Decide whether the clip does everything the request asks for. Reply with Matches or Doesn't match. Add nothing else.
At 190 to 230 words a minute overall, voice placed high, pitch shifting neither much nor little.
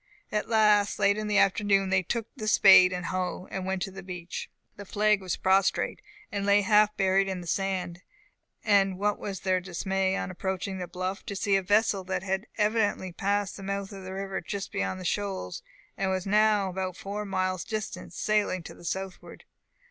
Doesn't match